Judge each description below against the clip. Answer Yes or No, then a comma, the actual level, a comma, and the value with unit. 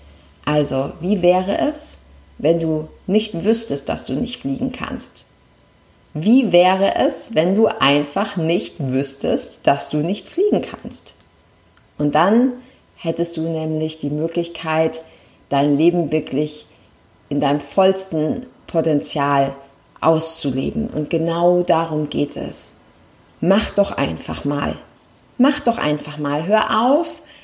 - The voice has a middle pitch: Yes, medium, 165 Hz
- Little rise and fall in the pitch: No, average, 5.1 semitones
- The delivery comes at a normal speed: No, slow, 120 wpm